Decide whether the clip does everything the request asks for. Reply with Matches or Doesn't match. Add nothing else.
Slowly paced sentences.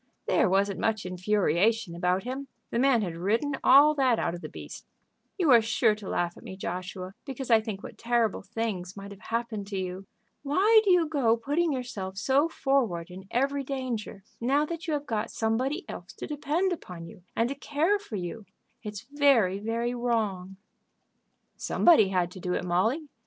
Doesn't match